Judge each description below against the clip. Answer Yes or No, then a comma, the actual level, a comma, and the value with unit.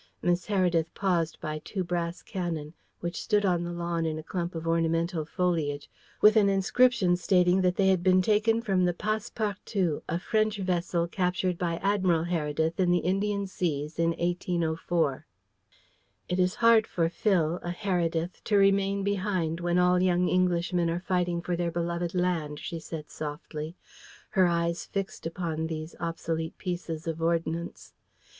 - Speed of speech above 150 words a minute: Yes, average, 160 wpm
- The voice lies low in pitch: No, medium, 175 Hz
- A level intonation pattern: Yes, narrow, 2.1 semitones